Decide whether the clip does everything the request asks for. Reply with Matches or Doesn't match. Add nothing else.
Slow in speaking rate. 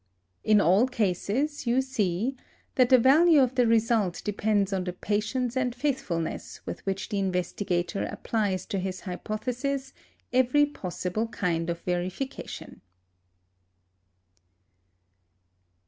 Matches